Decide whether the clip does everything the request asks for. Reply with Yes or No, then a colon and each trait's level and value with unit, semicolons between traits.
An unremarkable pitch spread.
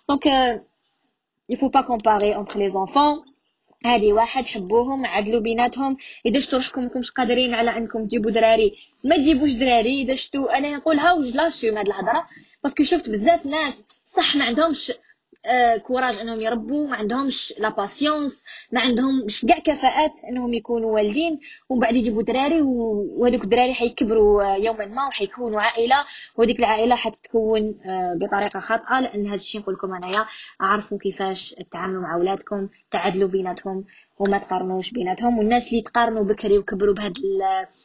Yes: average, 4.5 semitones